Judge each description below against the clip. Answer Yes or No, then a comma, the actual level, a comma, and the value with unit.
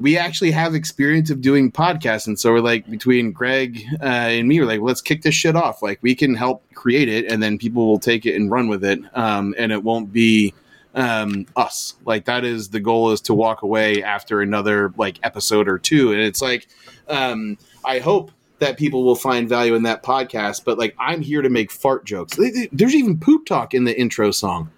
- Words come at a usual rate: No, fast, 225 wpm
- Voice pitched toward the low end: Yes, low, 115 Hz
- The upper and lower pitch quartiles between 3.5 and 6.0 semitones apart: Yes, average, 3.8 semitones